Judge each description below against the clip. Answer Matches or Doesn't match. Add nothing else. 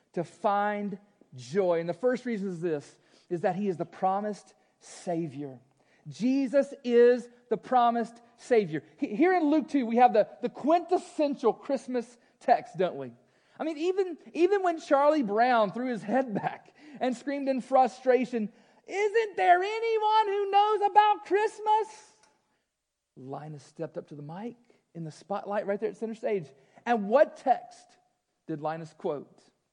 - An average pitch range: Doesn't match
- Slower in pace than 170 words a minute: Matches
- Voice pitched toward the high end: Matches